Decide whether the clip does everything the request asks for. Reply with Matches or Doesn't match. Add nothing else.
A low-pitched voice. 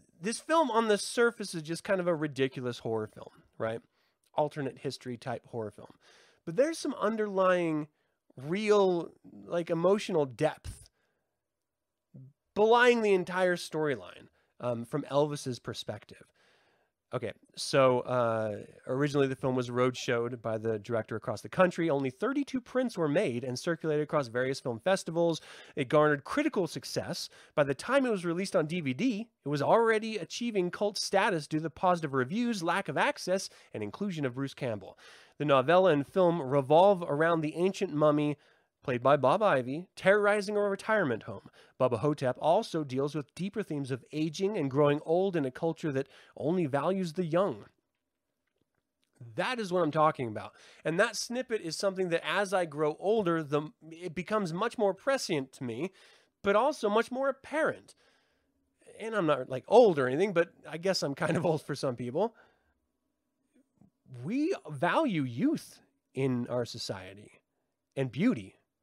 Doesn't match